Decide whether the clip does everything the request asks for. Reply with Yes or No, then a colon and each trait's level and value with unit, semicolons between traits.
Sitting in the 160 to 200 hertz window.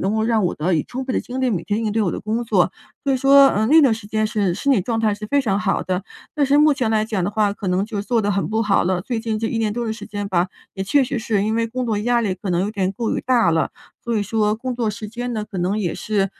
No: high, 215 Hz